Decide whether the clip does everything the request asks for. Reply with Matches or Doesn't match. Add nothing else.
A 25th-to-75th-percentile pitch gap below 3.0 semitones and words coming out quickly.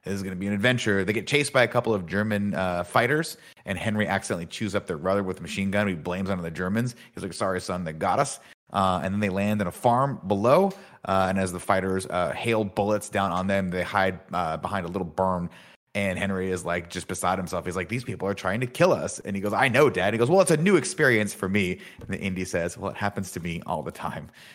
Matches